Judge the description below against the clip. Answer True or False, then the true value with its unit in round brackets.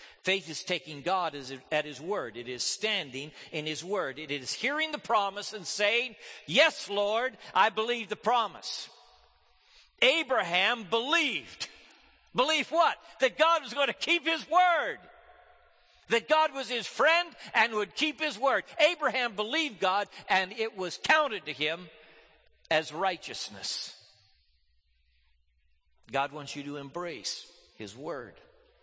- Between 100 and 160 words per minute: True (135 wpm)